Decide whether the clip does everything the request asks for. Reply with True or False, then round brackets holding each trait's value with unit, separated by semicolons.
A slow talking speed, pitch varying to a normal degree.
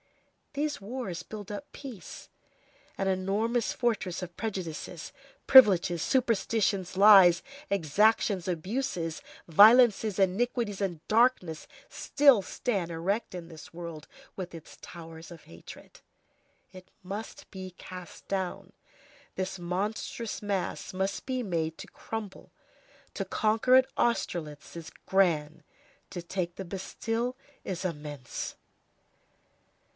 True (110 wpm; 4.4 semitones)